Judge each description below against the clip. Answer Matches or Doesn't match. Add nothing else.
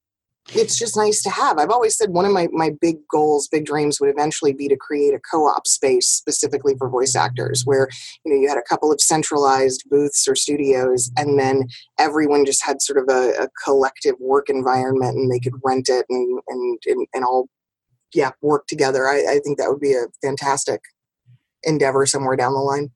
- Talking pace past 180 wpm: Matches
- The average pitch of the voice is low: Doesn't match